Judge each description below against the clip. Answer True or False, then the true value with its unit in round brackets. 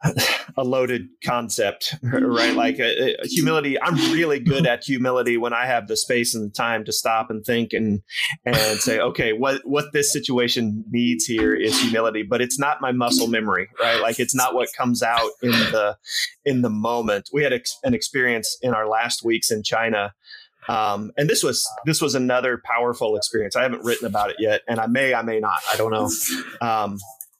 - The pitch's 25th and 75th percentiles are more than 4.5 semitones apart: False (2.4 semitones)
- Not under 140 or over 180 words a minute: False (195 wpm)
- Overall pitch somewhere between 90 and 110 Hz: False (120 Hz)